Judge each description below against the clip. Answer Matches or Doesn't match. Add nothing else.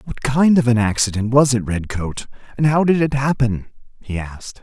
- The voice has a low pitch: Matches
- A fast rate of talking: Doesn't match